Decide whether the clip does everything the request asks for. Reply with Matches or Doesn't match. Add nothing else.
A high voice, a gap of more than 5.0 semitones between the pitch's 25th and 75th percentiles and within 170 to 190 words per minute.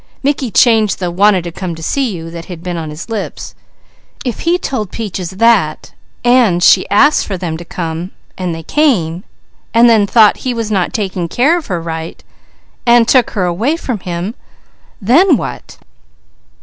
Matches